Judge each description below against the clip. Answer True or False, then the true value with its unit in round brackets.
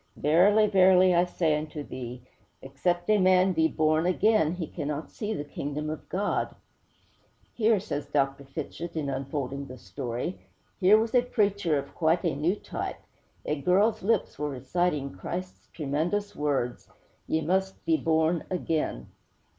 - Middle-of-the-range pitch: True (160 Hz)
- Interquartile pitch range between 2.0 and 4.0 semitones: False (4.5 semitones)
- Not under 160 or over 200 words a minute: False (150 wpm)